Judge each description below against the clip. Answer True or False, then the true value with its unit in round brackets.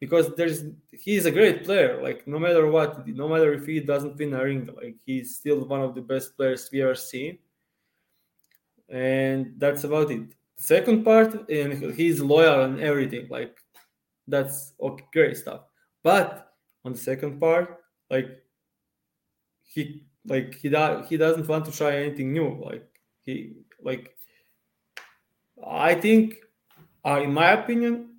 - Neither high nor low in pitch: True (150 Hz)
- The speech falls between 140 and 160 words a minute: True (150 wpm)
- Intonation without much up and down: False (3.7 semitones)